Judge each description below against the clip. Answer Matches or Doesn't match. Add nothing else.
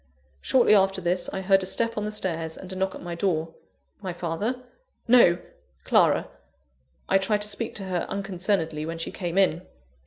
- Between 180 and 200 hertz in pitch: Matches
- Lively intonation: Doesn't match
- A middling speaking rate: Matches